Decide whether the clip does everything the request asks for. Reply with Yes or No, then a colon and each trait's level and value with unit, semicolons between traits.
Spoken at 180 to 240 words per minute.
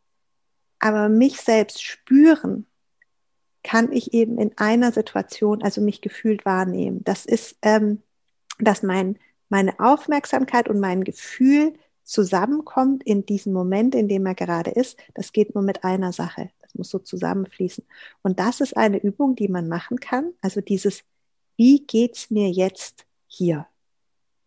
No: average, 145 wpm